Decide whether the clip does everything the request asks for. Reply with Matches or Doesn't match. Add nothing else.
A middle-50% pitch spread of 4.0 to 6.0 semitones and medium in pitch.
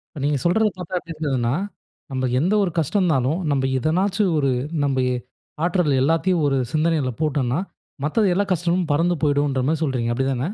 Matches